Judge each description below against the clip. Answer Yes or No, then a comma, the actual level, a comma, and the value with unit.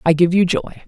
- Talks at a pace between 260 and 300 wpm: Yes, fast, 275 wpm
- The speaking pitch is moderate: Yes, medium, 175 Hz